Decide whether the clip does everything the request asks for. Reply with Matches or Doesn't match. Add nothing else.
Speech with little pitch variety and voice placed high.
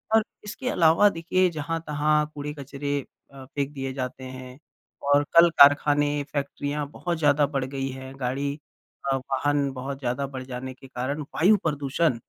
Doesn't match